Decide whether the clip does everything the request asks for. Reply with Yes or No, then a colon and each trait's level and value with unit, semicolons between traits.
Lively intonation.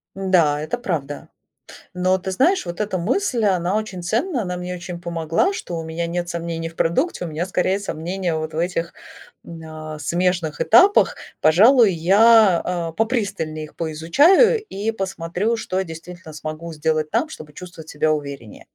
No: average, 3.9 semitones